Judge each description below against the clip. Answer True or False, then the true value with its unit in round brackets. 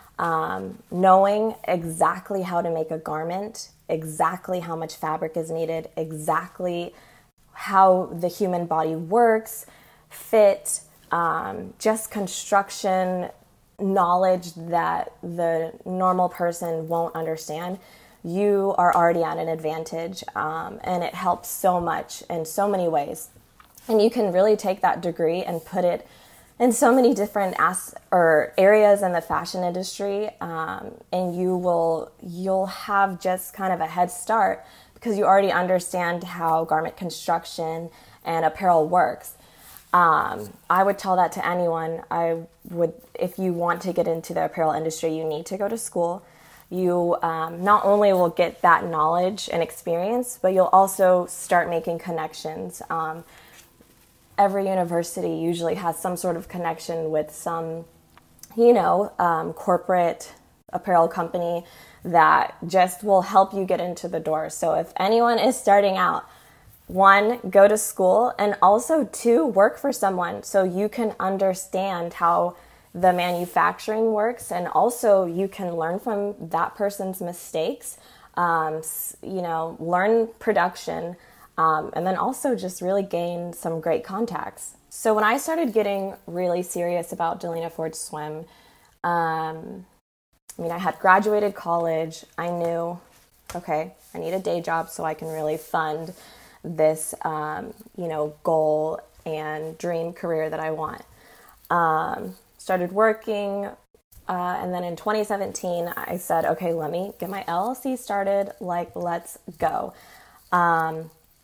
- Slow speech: False (145 wpm)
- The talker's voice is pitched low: False (175 Hz)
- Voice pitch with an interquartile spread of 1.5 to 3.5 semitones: True (3.1 semitones)